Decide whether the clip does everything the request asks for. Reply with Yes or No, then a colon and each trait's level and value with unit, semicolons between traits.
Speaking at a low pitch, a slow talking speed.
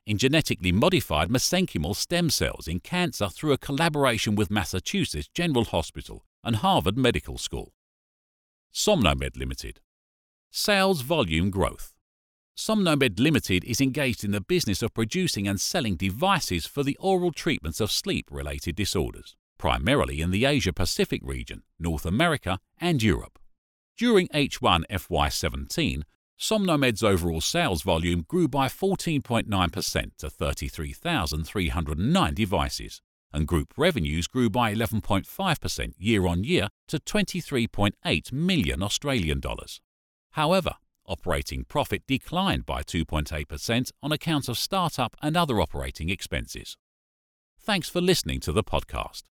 Yes: low, 100 Hz; slow, 125 wpm